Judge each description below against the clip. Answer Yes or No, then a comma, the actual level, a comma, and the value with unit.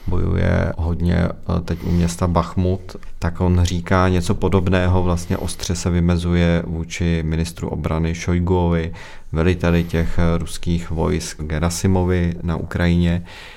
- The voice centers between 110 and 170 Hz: No, very low, 85 Hz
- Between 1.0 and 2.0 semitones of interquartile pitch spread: Yes, narrow, 1.4 semitones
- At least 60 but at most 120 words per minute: Yes, slow, 115 wpm